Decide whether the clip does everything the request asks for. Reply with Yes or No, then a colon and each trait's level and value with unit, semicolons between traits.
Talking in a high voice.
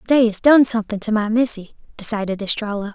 Yes: high, 220 Hz